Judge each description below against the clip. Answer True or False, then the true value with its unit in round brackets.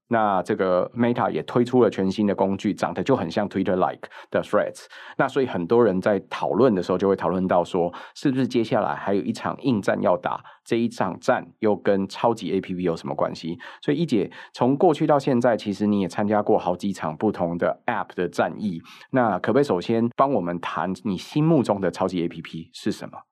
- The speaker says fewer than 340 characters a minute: False (365 characters per minute)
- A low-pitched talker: True (100 Hz)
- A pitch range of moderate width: True (4.4 semitones)